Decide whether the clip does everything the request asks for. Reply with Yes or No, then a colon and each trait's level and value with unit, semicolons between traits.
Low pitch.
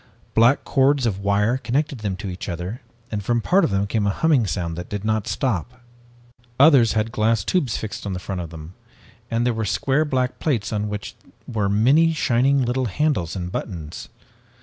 Yes: low, 110 Hz